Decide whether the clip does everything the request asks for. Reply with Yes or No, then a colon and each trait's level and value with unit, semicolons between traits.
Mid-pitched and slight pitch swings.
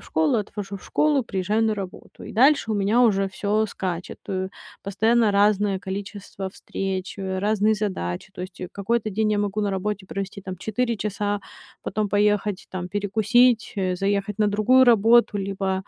No: high, 205 Hz; narrow, 2.0 semitones